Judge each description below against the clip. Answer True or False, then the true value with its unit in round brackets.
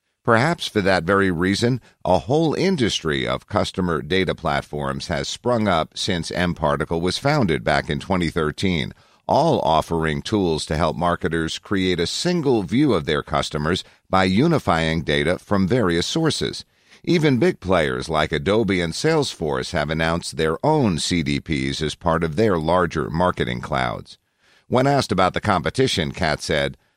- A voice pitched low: True (90 Hz)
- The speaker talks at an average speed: True (150 wpm)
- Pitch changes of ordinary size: False (6.9 semitones)